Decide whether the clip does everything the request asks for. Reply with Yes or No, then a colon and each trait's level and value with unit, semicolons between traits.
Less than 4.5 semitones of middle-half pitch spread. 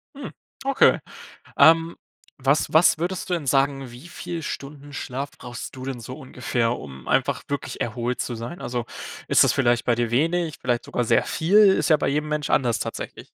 No: average, 4.8 semitones